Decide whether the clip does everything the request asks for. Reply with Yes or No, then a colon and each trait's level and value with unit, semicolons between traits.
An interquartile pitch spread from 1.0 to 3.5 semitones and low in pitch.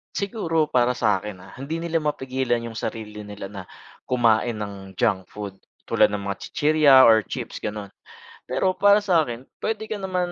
No: wide, 7.5 semitones; low, 120 Hz